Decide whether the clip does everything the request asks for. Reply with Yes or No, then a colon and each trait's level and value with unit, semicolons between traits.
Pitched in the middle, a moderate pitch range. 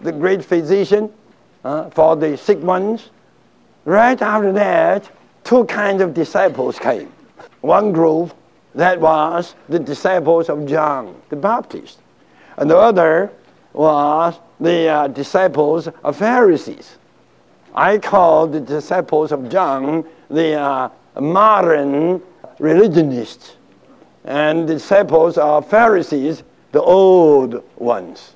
Yes: medium, 165 Hz; average, 4.0 semitones